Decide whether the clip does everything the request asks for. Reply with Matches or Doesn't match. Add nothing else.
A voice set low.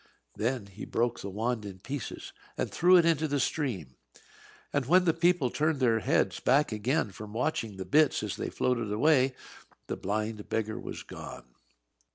Matches